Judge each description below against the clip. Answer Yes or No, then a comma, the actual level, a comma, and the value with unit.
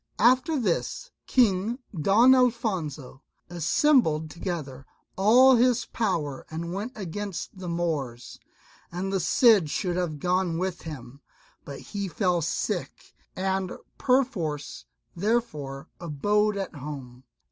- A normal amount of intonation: No, wide, 5.8 semitones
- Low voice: No, medium, 180 Hz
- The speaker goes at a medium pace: No, slow, 115 wpm